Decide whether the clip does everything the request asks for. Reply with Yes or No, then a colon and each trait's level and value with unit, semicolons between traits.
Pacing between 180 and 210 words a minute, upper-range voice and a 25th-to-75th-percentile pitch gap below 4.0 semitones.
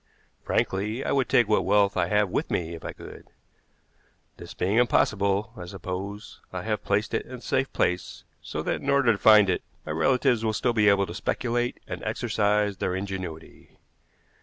No: average, 185 wpm; low, 105 Hz; average, 3.0 semitones